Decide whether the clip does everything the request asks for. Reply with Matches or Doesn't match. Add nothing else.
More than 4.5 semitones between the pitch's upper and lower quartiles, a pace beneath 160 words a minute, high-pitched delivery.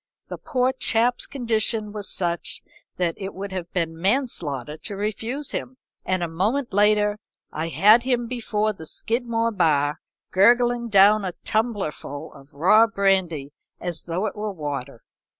Matches